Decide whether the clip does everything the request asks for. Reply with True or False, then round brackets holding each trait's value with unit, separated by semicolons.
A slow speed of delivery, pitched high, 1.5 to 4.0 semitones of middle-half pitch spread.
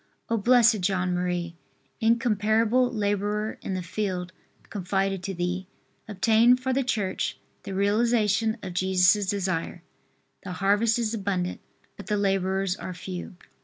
True (130 wpm; 200 Hz; 3.0 semitones)